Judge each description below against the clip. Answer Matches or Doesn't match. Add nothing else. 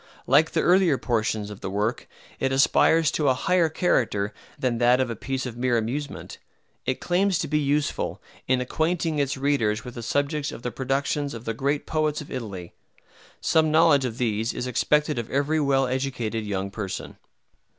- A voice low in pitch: Matches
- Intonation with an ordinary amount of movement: Matches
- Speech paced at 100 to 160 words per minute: Doesn't match